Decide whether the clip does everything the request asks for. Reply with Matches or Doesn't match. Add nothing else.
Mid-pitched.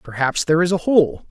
Matches